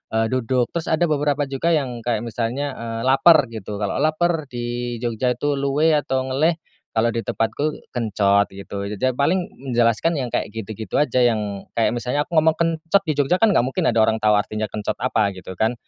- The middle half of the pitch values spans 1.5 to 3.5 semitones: No, average, 4.7 semitones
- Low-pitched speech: Yes, low, 120 Hz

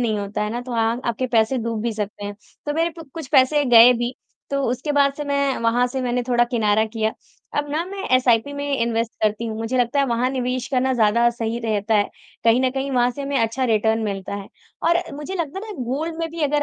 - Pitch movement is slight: No, average, 3.7 semitones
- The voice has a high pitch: Yes, high, 245 Hz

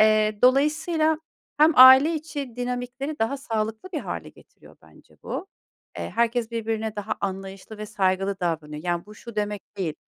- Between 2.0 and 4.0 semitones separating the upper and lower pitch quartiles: No, average, 4.9 semitones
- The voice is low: No, high, 225 Hz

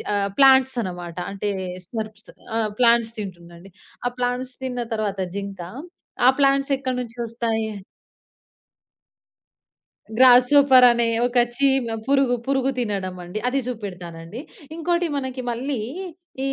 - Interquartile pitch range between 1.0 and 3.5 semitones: No, average, 4.6 semitones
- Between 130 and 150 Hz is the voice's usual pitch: No, high, 240 Hz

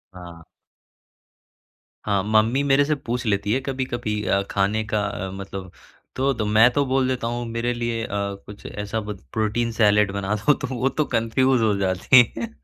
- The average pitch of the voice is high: No, low, 110 Hz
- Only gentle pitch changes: No, average, 3.4 semitones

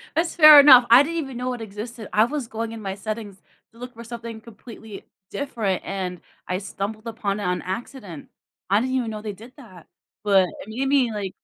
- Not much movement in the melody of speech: No, average, 3.7 semitones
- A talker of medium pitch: No, high, 225 Hz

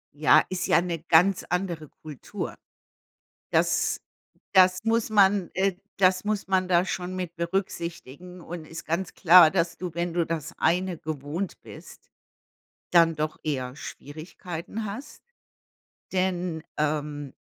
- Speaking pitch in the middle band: Yes, medium, 175 Hz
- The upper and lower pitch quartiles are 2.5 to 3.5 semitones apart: Yes, average, 2.8 semitones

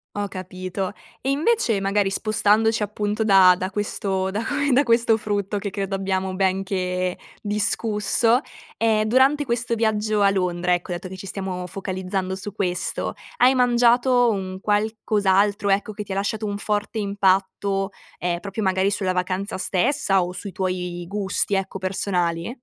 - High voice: Yes, high, 200 Hz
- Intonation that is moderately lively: No, narrow, 2.3 semitones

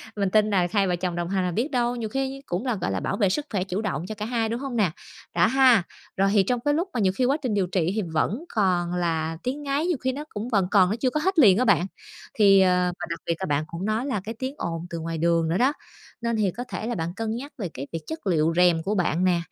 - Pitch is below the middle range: No, high, 200 Hz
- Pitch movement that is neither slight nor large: No, wide, 5.8 semitones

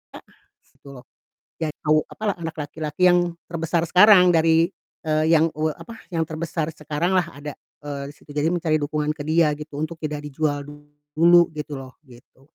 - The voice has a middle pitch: Yes, medium, 155 Hz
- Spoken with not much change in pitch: Yes, narrow, 2.1 semitones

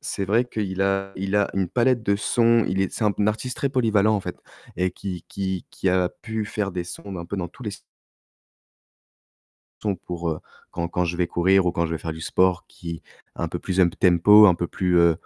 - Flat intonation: No, average, 3.0 semitones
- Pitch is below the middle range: Yes, very low, 95 Hz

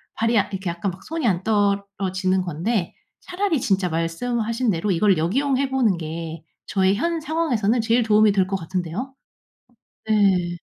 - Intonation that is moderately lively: Yes, average, 4.5 semitones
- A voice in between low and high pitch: No, high, 200 Hz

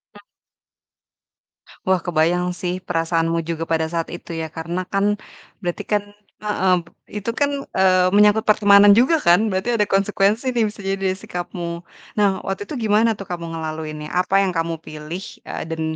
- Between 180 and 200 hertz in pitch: Yes, medium, 185 Hz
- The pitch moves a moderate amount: Yes, average, 3.7 semitones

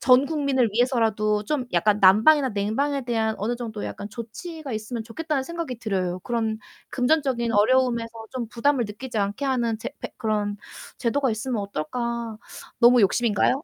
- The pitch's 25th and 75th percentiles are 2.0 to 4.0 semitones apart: Yes, average, 3.6 semitones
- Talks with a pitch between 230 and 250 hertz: Yes, high, 235 Hz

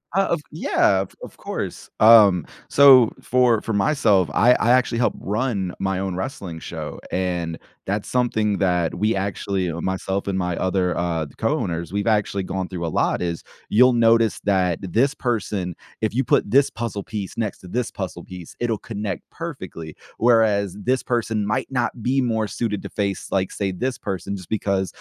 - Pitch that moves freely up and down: No, average, 3.8 semitones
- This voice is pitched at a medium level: No, low, 100 Hz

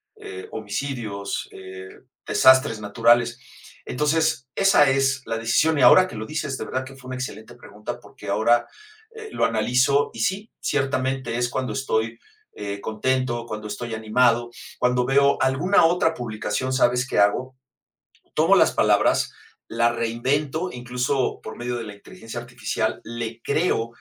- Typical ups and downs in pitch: Yes, average, 3.0 semitones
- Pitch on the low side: Yes, low, 125 Hz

